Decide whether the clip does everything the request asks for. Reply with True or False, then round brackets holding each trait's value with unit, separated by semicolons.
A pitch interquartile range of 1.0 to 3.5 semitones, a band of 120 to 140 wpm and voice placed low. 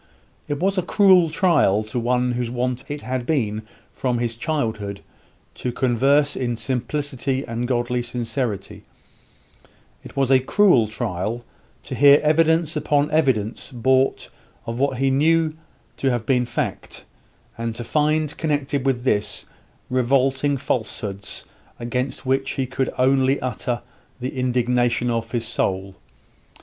True (3.0 semitones; 135 wpm; 130 Hz)